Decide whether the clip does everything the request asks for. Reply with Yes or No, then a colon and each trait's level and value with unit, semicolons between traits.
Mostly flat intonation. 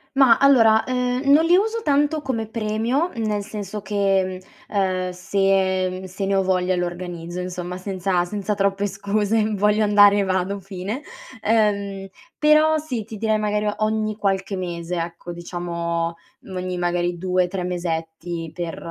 No: average, 3.2 semitones